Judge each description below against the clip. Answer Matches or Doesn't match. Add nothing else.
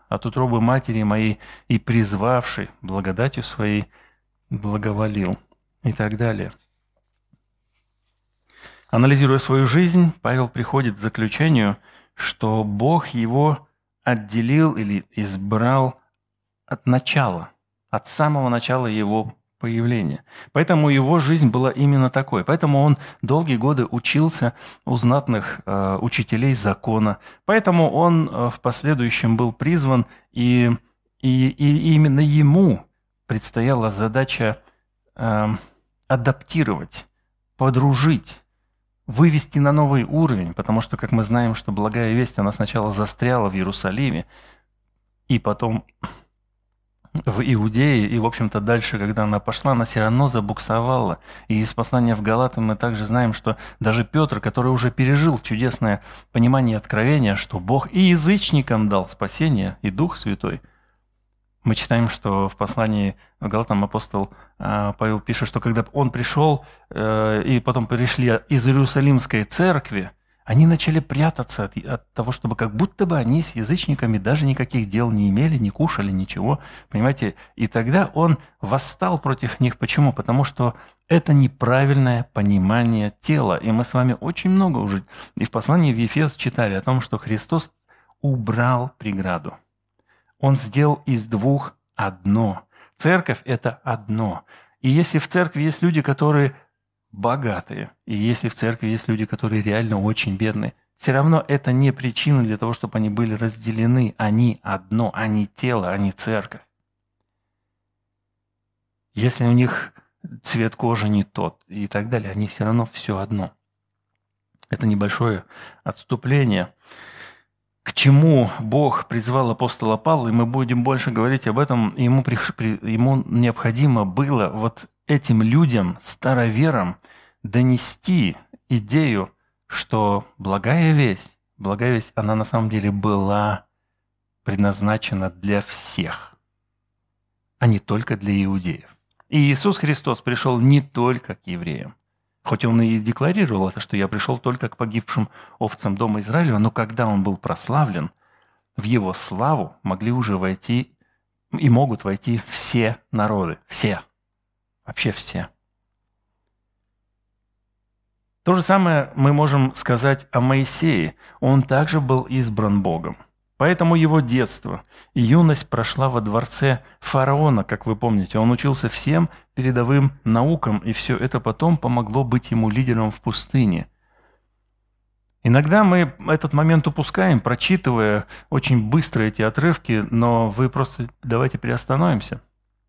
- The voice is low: Matches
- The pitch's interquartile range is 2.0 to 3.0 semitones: Doesn't match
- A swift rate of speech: Doesn't match